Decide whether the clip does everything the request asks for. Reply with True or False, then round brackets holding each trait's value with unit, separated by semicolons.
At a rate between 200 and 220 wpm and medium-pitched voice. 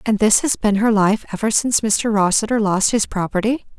False (205 wpm; 215 Hz)